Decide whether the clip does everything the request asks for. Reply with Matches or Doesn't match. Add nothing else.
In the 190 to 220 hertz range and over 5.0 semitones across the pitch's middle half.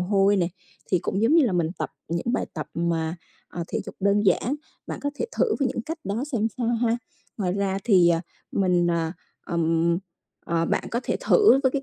Matches